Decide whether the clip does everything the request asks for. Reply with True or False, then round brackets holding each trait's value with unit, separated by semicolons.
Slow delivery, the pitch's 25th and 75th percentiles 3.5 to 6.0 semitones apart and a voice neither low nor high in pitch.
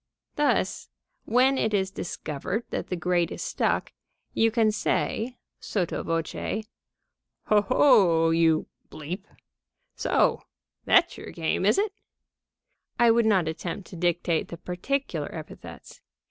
False (120 wpm; 5.3 semitones; 195 Hz)